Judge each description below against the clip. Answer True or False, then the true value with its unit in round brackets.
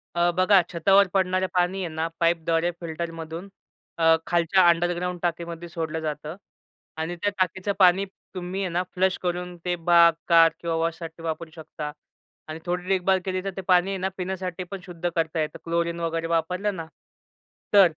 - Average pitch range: False (2.0 semitones)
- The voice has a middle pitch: True (175 Hz)